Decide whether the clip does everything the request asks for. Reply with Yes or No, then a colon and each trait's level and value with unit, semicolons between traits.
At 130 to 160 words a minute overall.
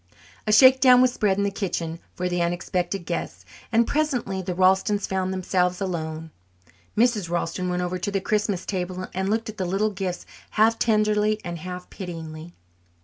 No: average, 170 wpm